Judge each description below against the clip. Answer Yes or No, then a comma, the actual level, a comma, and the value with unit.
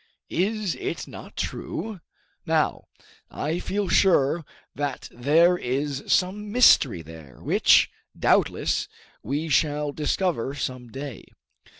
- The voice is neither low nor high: Yes, medium, 145 Hz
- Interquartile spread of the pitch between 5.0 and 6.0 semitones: Yes, wide, 5.5 semitones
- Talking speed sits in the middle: No, slow, 105 wpm